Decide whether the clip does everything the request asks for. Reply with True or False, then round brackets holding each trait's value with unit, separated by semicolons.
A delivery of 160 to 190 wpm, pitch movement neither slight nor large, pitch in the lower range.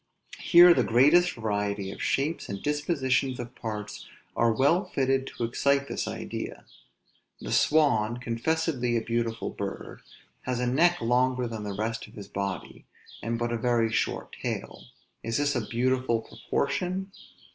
False (150 wpm; 3.6 semitones; 125 Hz)